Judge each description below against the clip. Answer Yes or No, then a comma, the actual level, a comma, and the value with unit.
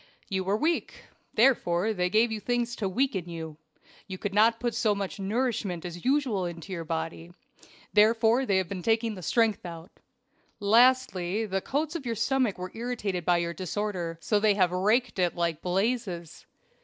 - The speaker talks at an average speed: Yes, average, 170 wpm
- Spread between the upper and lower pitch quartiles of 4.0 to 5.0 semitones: Yes, average, 4.5 semitones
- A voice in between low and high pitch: No, high, 205 Hz